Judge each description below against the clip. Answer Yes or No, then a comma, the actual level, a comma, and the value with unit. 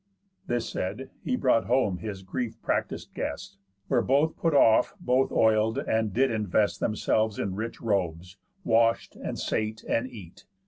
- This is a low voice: Yes, low, 110 Hz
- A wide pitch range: No, average, 3.5 semitones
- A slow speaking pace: No, average, 150 wpm